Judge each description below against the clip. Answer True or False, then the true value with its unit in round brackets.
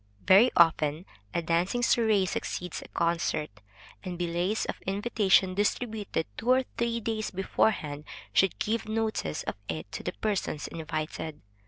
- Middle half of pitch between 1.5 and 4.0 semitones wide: False (5.1 semitones)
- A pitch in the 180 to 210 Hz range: True (185 Hz)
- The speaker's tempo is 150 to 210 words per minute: False (140 wpm)